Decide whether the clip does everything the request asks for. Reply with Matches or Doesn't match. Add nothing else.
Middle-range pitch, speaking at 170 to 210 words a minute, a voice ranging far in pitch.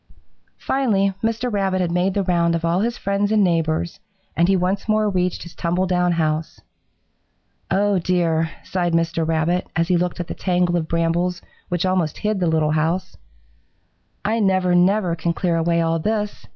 Doesn't match